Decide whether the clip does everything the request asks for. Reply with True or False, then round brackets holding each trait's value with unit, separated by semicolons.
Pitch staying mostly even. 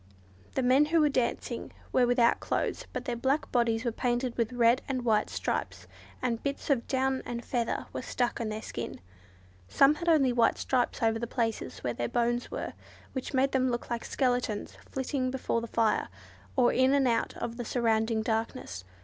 True (2.3 semitones)